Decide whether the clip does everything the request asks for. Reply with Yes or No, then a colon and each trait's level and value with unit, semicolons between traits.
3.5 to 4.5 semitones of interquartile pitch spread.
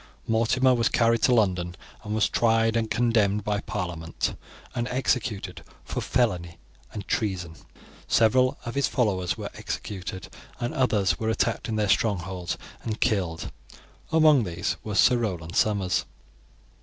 Yes: average, 4.1 semitones